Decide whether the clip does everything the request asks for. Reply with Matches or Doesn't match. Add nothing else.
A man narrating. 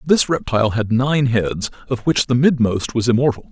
Matches